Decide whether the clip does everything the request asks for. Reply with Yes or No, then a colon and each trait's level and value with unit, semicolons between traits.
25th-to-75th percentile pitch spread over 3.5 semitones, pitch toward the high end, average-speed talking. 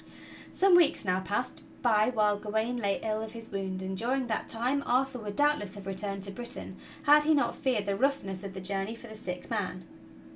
No: average, 4.2 semitones; high, 215 Hz; fast, 215 wpm